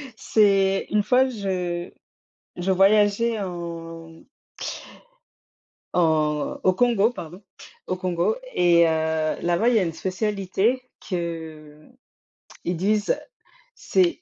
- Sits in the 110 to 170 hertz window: No, medium, 185 Hz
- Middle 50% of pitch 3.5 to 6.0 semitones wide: Yes, average, 4.0 semitones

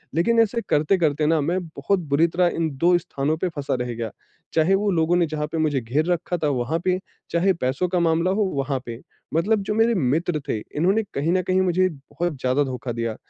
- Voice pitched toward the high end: No, medium, 165 Hz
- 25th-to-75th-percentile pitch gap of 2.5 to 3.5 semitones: No, average, 4.4 semitones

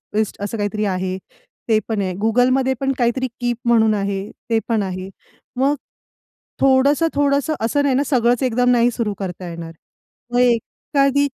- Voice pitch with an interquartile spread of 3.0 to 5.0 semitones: Yes, average, 4.3 semitones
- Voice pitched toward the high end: Yes, high, 235 Hz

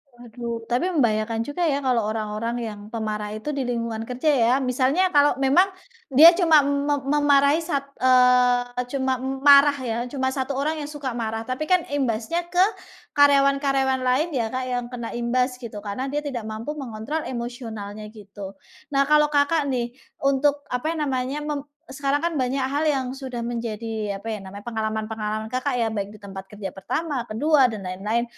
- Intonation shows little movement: No, average, 4.1 semitones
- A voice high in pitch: Yes, very high, 255 Hz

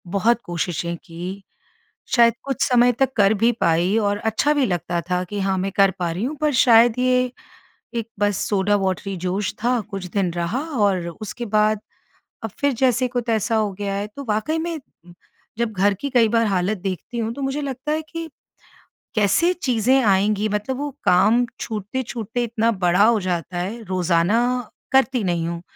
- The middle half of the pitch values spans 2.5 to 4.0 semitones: No, average, 4.4 semitones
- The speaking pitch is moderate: No, high, 215 Hz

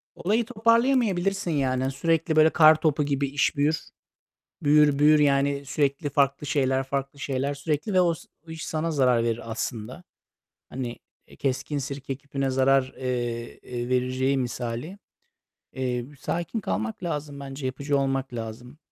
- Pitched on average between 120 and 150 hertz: Yes, medium, 140 Hz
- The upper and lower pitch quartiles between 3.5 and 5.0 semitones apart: No, average, 3.1 semitones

